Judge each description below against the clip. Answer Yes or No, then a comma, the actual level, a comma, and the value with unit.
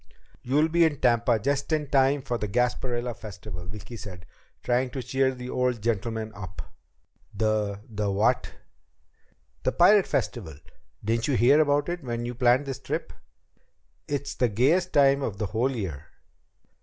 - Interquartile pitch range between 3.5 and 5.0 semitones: Yes, average, 4.2 semitones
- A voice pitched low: Yes, low, 120 Hz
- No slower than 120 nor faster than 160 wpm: Yes, average, 155 wpm